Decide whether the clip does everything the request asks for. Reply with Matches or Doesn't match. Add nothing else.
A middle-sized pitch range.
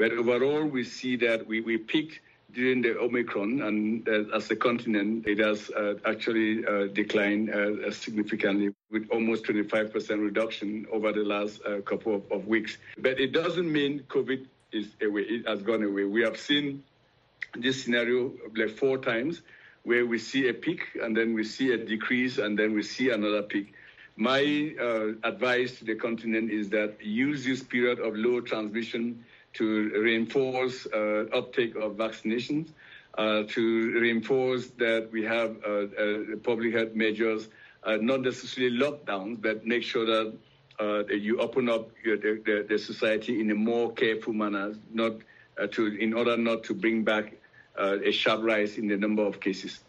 Doesn't match